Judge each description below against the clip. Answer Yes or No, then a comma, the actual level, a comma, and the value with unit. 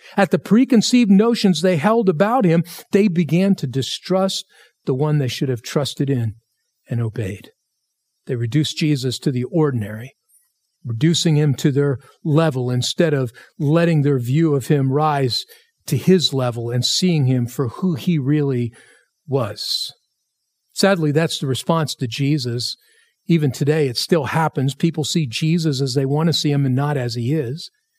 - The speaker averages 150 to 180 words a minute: Yes, average, 165 wpm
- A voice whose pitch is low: No, medium, 150 Hz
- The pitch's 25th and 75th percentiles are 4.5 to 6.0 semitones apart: Yes, average, 4.8 semitones